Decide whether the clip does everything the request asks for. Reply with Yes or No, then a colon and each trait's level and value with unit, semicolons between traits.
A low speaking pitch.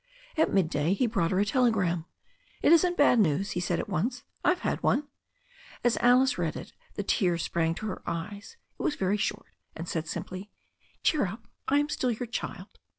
No: high, 205 Hz